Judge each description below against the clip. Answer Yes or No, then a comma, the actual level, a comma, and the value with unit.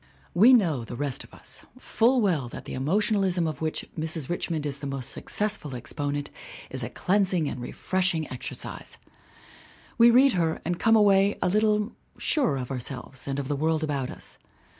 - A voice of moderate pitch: Yes, medium, 160 Hz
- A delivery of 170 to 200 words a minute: Yes, average, 180 wpm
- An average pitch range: No, wide, 6.4 semitones